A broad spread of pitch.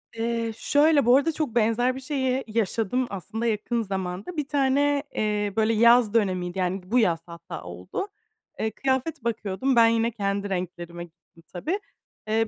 No: average, 5.0 semitones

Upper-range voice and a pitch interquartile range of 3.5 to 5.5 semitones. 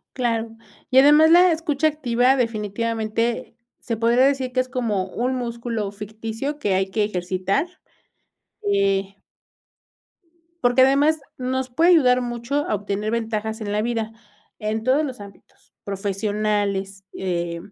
Yes: high, 230 Hz; average, 4.0 semitones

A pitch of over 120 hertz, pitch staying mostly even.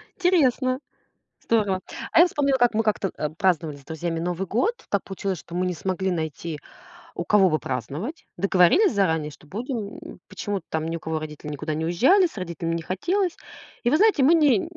No: high, 190 Hz; wide, 7.9 semitones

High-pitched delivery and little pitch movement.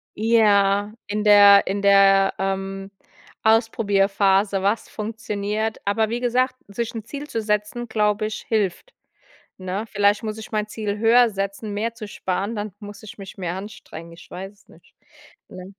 Yes: high, 205 Hz; narrow, 2.0 semitones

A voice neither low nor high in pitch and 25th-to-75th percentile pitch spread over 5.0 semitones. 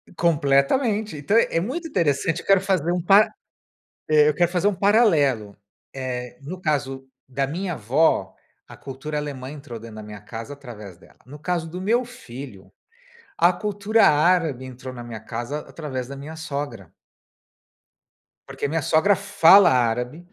Yes: medium, 150 Hz; wide, 5.6 semitones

